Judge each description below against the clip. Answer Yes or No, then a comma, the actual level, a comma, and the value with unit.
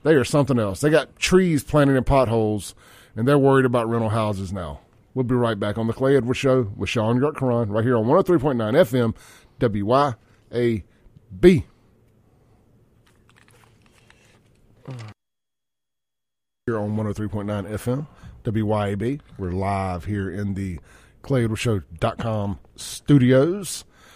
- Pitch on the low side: Yes, low, 115 Hz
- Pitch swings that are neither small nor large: Yes, average, 3.7 semitones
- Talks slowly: Yes, slow, 115 wpm